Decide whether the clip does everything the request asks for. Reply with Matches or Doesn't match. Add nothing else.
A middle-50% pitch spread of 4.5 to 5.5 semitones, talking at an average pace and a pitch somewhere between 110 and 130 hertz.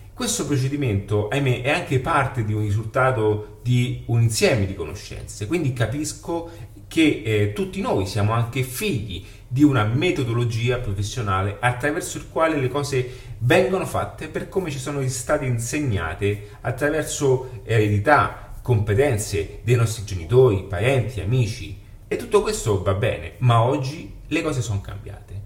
Matches